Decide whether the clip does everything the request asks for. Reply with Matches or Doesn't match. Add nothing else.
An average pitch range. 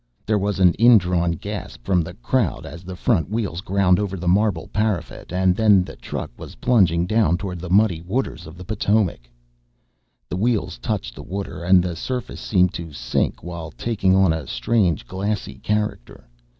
Matches